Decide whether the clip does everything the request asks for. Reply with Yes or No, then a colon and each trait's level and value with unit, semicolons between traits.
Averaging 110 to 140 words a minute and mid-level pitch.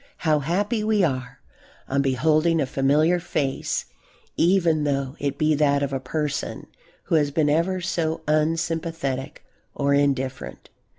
Yes: slow, 135 wpm; medium, 150 Hz